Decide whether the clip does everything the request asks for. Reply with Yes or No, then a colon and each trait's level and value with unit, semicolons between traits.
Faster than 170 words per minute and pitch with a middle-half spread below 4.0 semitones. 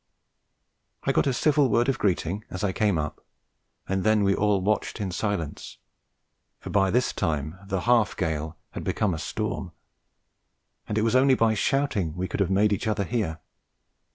Yes: average, 180 wpm; average, 3.3 semitones